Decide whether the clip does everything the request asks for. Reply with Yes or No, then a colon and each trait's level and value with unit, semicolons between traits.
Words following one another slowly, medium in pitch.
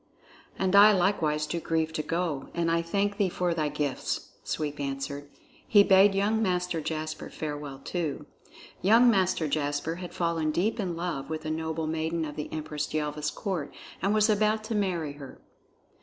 No: average, 170 wpm; medium, 165 Hz